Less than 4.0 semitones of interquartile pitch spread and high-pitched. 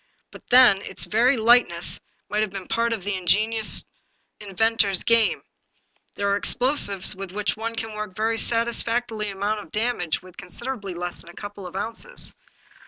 Yes: average, 2.8 semitones; high, 215 Hz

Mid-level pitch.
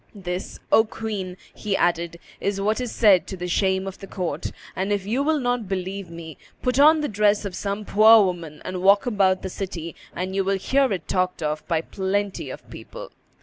No: high, 195 Hz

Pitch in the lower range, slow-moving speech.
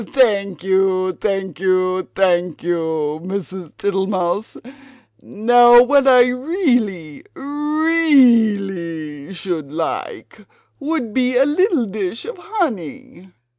No: high, 200 Hz; slow, 95 wpm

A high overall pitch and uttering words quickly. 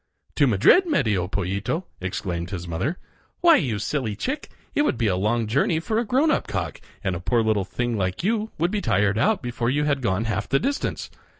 No: low, 120 Hz; fast, 210 wpm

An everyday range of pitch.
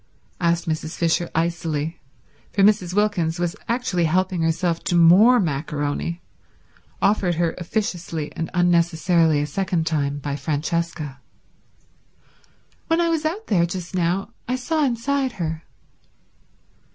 Yes: average, 3.4 semitones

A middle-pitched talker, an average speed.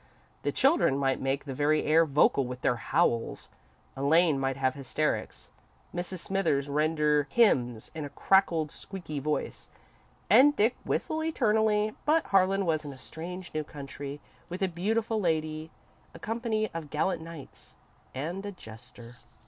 Yes: medium, 160 Hz; average, 150 wpm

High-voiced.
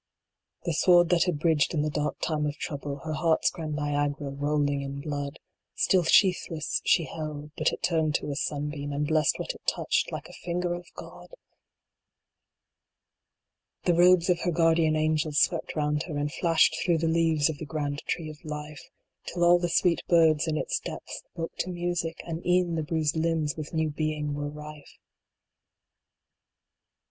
No: medium, 155 Hz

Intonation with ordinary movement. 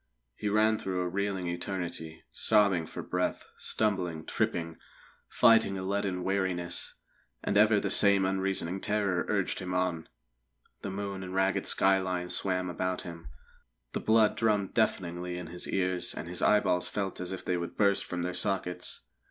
No: narrow, 2.0 semitones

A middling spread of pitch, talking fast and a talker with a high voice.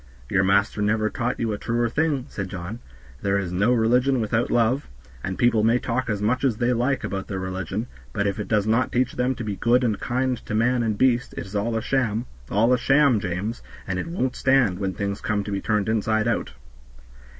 No: average, 3.6 semitones; fast, 225 wpm; low, 110 Hz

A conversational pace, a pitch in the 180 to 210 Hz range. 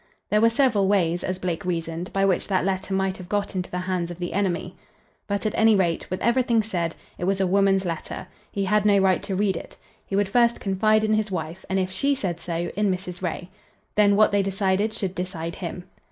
No: fast, 225 wpm; high, 190 Hz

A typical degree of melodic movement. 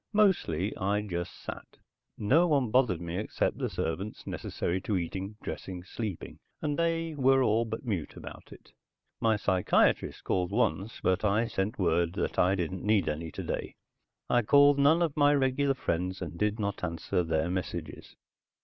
No: wide, 6.7 semitones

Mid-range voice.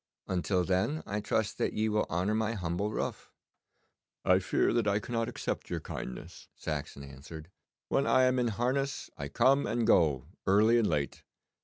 No: low, 105 Hz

